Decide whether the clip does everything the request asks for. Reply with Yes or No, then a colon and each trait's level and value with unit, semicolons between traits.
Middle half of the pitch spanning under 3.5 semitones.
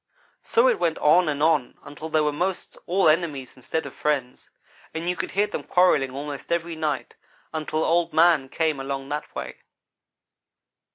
Yes: average, 2.9 semitones